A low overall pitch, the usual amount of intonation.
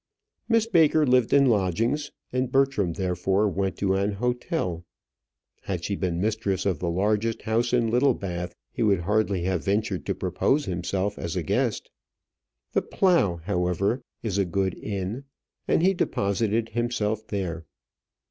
Yes: low, 105 Hz; average, 4.4 semitones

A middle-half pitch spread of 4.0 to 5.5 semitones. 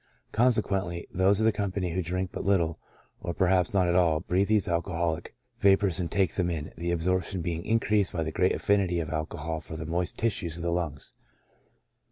No: average, 2.7 semitones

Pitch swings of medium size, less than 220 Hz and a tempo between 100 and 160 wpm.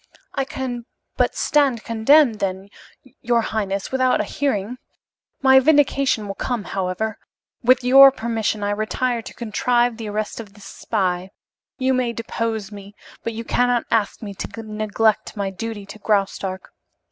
No: average, 3.3 semitones; high, 225 Hz; average, 150 wpm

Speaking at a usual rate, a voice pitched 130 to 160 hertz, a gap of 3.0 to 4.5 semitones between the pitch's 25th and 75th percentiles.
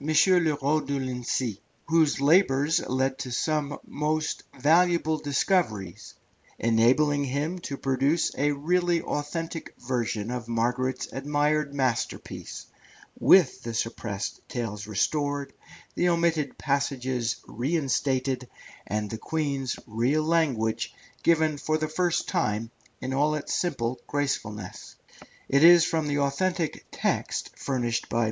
No: slow, 120 wpm; medium, 140 Hz; average, 3.9 semitones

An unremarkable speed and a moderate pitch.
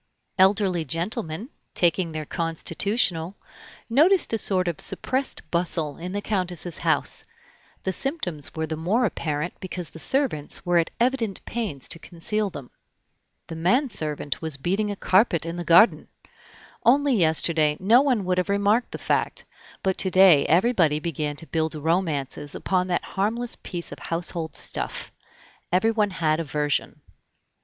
Yes: average, 150 wpm; medium, 180 Hz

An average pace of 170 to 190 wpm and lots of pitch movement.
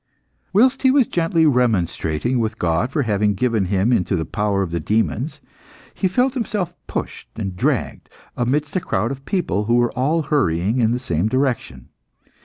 Yes: average, 175 wpm; wide, 7.3 semitones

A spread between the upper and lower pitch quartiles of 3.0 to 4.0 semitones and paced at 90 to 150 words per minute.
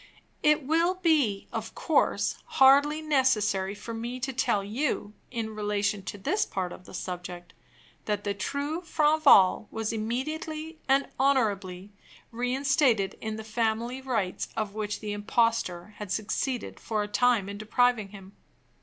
No: average, 4.7 semitones; average, 145 wpm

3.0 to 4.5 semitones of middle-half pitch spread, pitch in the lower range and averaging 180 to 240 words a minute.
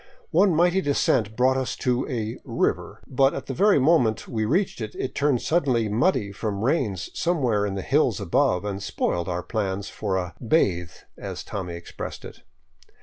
No: wide, 5.6 semitones; low, 115 Hz; average, 185 wpm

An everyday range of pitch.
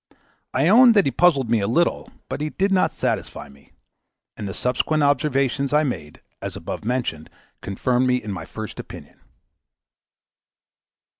No: wide, 5.9 semitones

